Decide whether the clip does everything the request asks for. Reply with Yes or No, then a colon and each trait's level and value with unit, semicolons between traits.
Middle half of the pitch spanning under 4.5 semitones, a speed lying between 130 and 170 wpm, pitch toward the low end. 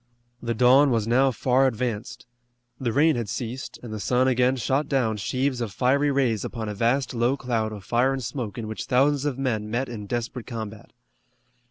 No: average, 2.9 semitones; average, 195 wpm; low, 125 Hz